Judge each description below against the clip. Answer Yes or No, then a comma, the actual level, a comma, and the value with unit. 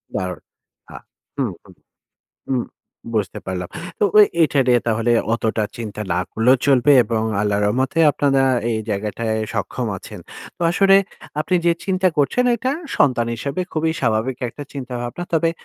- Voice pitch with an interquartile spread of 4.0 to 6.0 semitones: Yes, average, 5.2 semitones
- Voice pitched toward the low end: Yes, low, 125 Hz